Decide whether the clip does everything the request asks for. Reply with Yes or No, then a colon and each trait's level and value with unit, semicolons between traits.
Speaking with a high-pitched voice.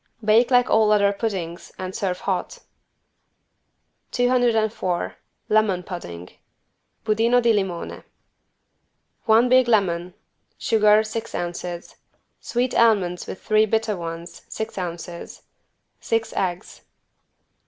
Yes: high, 210 Hz